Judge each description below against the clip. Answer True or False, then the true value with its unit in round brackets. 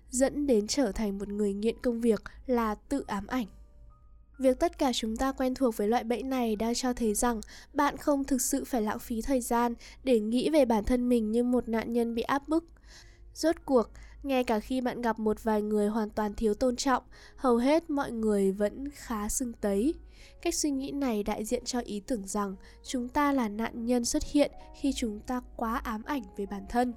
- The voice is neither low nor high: False (245 Hz)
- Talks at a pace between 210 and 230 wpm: True (220 wpm)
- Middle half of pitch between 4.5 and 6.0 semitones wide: False (3.4 semitones)